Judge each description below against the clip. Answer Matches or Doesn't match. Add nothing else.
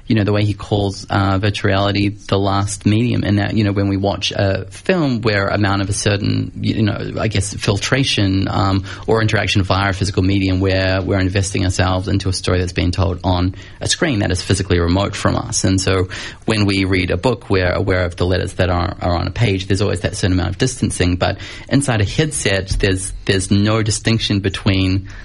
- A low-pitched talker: Matches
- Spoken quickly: Matches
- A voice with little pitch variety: Matches